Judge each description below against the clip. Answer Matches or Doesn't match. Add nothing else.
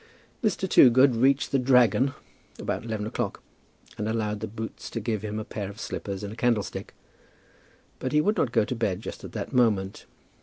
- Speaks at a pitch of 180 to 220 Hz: Doesn't match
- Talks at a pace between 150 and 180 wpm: Doesn't match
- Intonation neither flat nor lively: Matches